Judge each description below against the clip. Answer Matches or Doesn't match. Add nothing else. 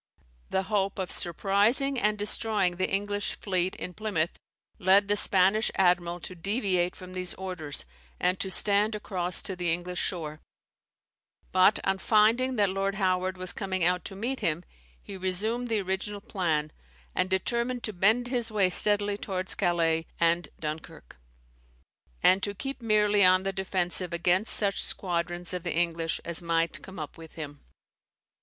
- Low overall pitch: Doesn't match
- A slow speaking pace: Doesn't match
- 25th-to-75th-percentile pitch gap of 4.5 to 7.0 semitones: Doesn't match